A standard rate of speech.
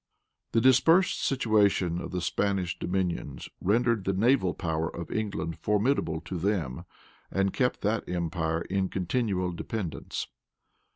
No: slow, 125 wpm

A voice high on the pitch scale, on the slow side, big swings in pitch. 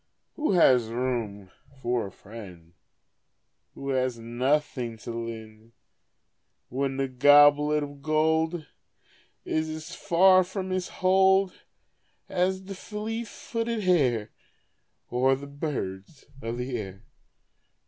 No: medium, 140 Hz; slow, 110 wpm; wide, 7.3 semitones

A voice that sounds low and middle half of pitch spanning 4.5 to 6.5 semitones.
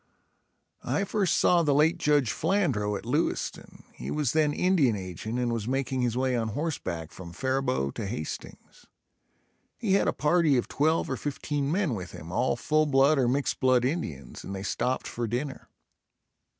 Yes: low, 130 Hz; average, 5.2 semitones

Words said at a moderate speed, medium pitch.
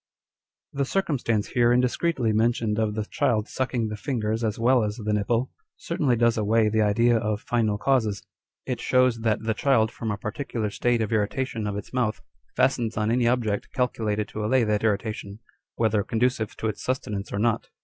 No: average, 180 wpm; low, 115 Hz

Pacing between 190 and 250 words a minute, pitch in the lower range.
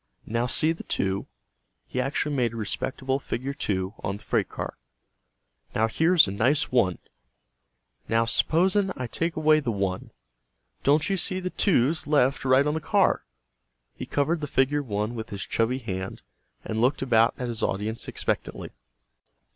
No: average, 165 wpm; low, 130 Hz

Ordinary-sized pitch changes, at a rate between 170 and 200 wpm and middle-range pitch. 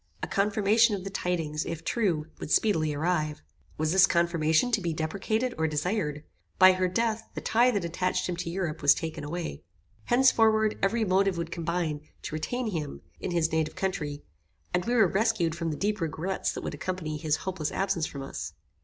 Yes: average, 4.2 semitones; average, 190 wpm; medium, 180 Hz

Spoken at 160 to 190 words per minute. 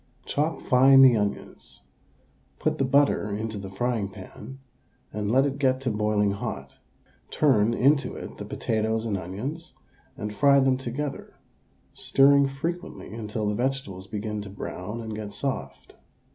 No: average, 145 wpm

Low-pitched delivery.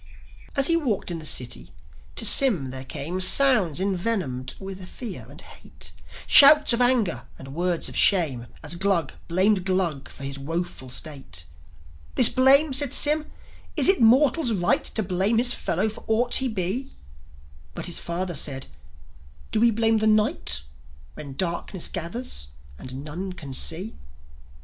No: medium, 185 Hz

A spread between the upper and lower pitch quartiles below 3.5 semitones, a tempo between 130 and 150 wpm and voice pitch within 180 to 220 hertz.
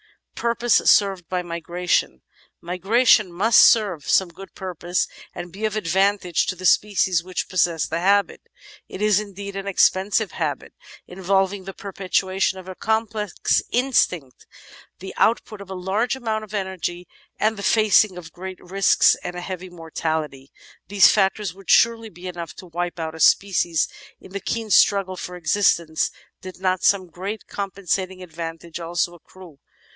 No: narrow, 2.5 semitones; average, 160 wpm; medium, 185 Hz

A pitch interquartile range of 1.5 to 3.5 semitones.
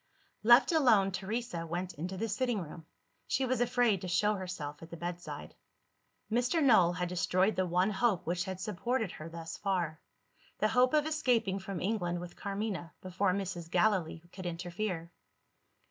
No: average, 4.1 semitones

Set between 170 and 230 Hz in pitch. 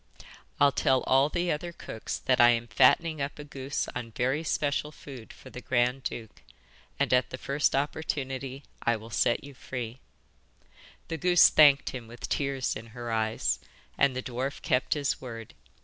No: low, 130 Hz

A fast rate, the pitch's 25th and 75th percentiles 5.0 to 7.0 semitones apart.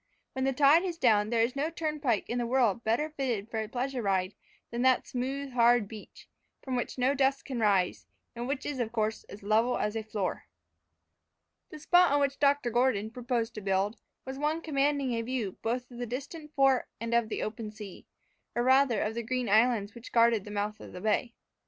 No: fast, 210 wpm; average, 3.7 semitones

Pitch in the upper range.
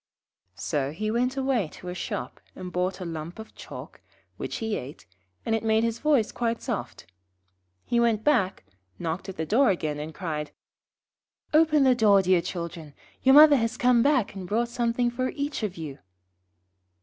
Yes: high, 220 Hz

